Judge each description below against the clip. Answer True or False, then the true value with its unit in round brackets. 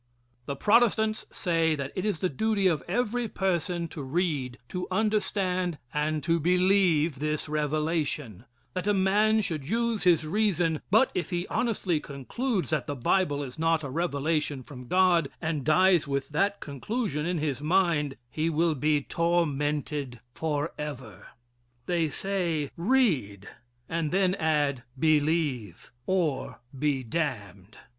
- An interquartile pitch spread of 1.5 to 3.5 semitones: False (4.3 semitones)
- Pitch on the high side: False (160 Hz)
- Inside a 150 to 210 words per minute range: False (135 wpm)